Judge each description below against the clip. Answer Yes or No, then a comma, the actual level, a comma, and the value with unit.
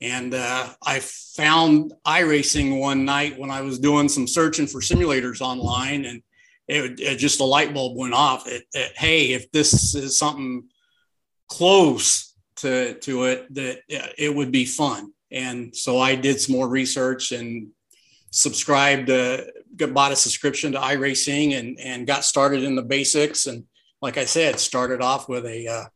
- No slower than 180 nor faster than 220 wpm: No, average, 170 wpm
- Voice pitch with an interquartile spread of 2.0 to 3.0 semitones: Yes, narrow, 2.4 semitones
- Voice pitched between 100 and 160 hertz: Yes, low, 135 Hz